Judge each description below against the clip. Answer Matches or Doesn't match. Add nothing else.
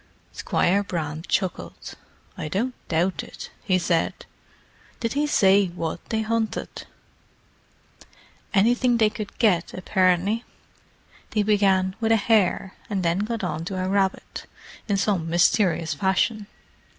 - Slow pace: Matches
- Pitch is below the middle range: Doesn't match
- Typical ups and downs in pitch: Matches